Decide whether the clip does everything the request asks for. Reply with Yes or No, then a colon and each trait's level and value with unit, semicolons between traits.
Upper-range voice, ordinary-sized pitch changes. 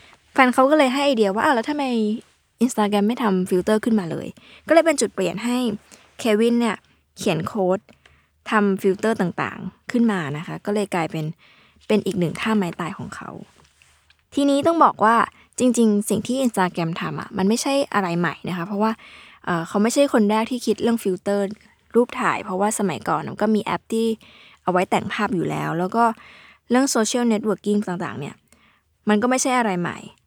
Yes: high, 215 Hz; average, 3.8 semitones